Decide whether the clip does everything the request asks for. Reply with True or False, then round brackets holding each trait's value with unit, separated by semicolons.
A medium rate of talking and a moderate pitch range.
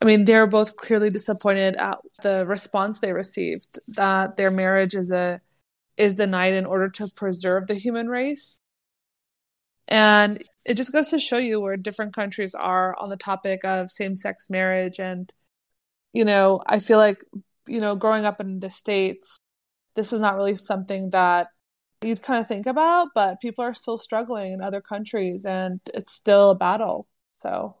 False (175 wpm; 2.3 semitones)